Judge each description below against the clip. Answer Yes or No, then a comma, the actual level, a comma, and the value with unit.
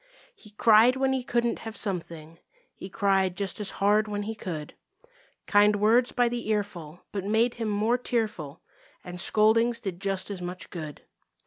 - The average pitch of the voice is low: No, high, 210 Hz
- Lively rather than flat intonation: No, average, 3.6 semitones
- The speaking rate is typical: Yes, average, 165 wpm